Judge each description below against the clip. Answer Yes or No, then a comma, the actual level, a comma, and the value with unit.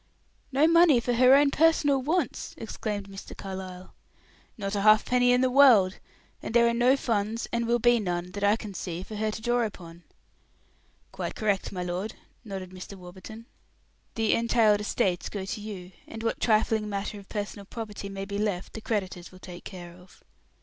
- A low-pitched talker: No, high, 210 Hz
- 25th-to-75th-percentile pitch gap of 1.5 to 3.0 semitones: No, average, 3.6 semitones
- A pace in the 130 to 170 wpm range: No, average, 185 wpm